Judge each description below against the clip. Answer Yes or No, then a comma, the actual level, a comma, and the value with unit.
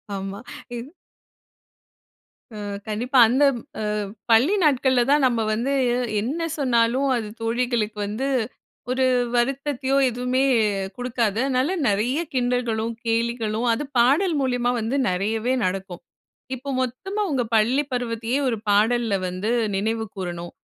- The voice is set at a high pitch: Yes, high, 240 Hz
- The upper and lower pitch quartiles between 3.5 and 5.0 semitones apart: No, average, 3.0 semitones